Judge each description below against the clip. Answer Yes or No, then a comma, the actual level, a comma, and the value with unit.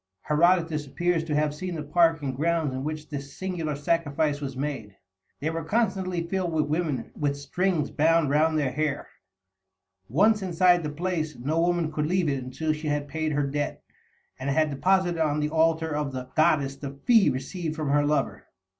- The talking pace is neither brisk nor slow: Yes, average, 185 wpm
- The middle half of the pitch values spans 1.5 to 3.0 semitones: Yes, average, 2.7 semitones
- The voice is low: No, medium, 155 Hz